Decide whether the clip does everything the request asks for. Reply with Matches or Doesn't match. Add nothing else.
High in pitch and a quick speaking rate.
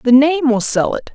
Matches